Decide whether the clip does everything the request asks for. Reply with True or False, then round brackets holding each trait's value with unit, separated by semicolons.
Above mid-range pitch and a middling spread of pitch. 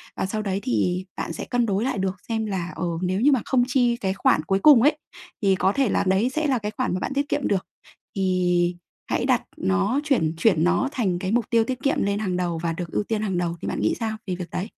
True (195 Hz; 4.7 semitones)